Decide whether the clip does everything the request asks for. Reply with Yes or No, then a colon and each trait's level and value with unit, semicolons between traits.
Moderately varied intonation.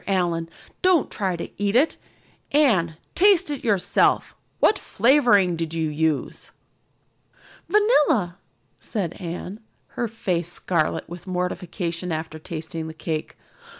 No: wide, 6.0 semitones